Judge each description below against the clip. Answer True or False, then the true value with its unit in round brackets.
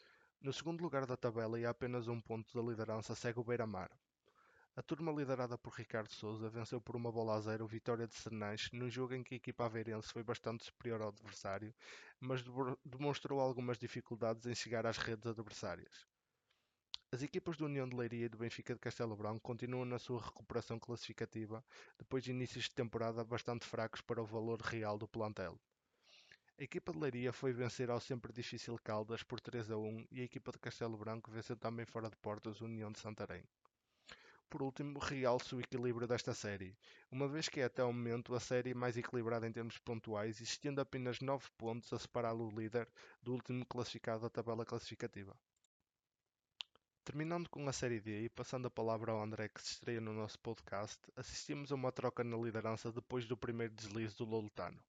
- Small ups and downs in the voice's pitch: True (2.0 semitones)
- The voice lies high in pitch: False (120 Hz)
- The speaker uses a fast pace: True (190 wpm)